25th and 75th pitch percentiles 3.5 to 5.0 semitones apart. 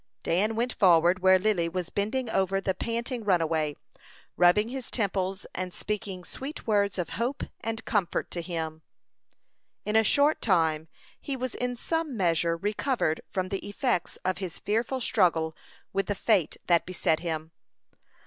Yes: average, 4.6 semitones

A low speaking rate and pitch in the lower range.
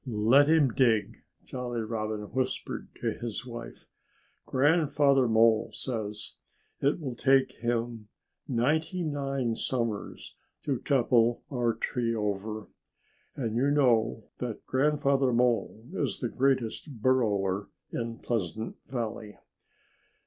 Yes: slow, 110 wpm; low, 120 Hz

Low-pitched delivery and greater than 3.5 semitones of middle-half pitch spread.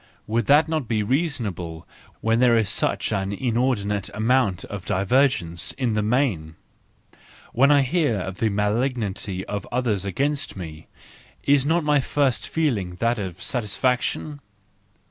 Yes: low, 115 Hz; average, 5.3 semitones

